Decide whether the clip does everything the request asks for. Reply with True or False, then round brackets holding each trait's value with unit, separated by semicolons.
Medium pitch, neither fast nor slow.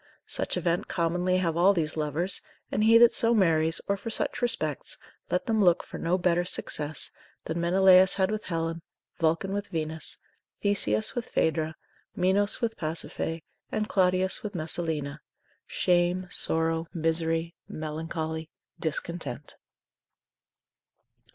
False (170 Hz; 130 wpm)